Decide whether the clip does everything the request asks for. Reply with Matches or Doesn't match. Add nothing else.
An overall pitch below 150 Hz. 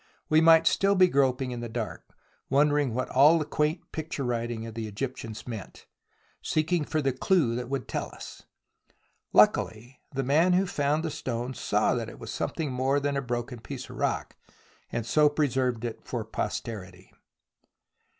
Matches